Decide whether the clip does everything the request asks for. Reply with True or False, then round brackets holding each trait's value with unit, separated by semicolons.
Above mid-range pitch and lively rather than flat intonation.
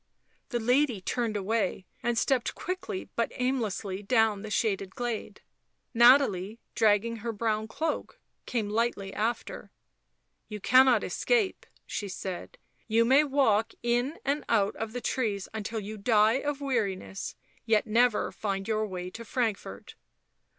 False (225 Hz; 3.1 semitones)